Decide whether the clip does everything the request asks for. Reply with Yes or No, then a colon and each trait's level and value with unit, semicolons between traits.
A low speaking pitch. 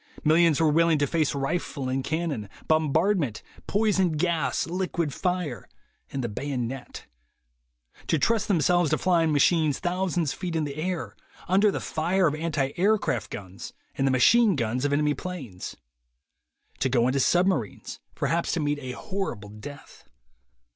No: medium, 155 Hz